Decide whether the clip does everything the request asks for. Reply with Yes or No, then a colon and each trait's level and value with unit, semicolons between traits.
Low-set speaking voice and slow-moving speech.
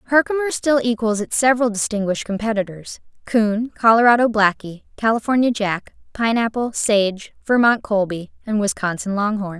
No: high, 220 Hz; slow, 120 wpm